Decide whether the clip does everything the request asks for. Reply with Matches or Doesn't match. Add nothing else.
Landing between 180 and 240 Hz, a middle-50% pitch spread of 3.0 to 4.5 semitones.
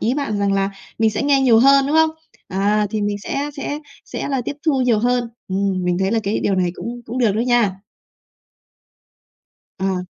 Doesn't match